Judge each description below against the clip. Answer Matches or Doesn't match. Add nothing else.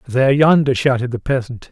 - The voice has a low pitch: Matches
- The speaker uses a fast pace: Doesn't match